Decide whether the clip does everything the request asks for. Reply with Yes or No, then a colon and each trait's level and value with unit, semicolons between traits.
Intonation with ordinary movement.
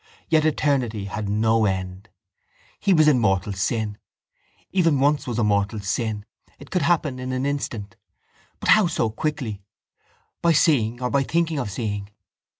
No: wide, 6.1 semitones